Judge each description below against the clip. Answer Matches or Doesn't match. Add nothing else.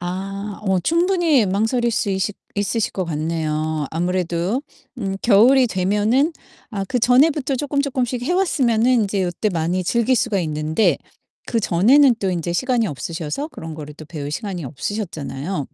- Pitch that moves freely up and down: Matches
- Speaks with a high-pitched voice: Matches